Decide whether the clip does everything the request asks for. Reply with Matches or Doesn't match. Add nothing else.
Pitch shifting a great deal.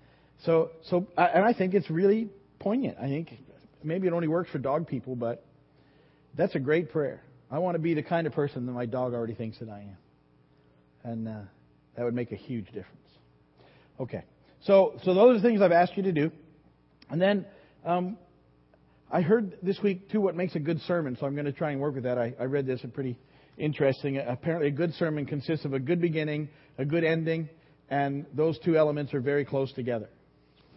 Matches